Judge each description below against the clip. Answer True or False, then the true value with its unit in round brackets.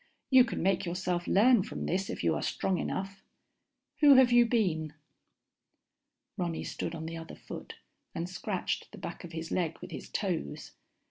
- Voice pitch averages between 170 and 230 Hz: True (185 Hz)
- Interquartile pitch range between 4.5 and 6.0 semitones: True (4.8 semitones)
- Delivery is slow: False (175 wpm)